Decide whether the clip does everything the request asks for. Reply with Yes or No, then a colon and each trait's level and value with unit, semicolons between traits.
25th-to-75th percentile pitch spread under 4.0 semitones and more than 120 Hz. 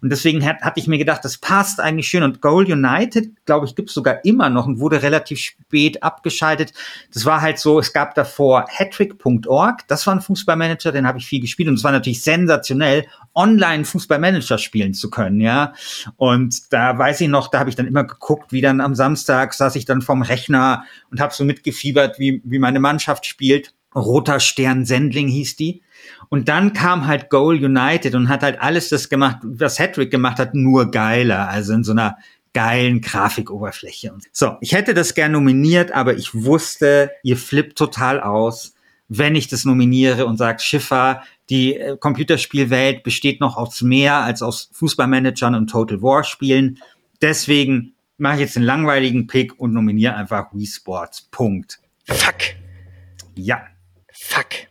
Yes: average, 3.4 semitones; low, 135 Hz